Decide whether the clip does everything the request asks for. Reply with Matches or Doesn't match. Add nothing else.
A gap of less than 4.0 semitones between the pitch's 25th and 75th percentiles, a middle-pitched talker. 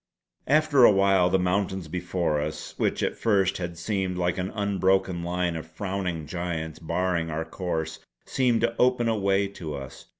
Doesn't match